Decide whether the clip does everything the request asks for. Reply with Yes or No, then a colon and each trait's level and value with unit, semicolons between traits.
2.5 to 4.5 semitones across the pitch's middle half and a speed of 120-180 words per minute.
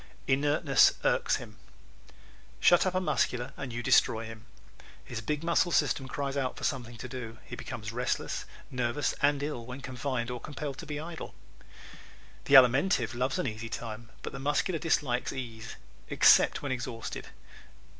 Yes: average, 3.7 semitones; average, 165 wpm